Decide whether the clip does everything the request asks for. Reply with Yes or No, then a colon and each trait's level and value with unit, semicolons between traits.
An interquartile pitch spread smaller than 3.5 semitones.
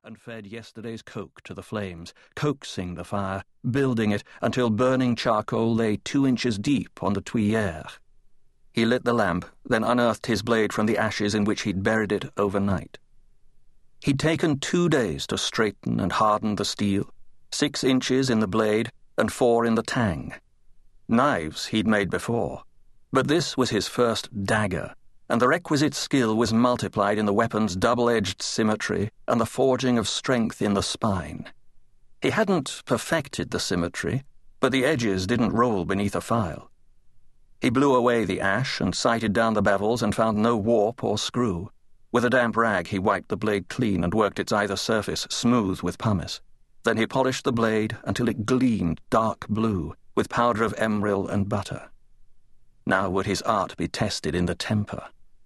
Yes: average, 3.1 semitones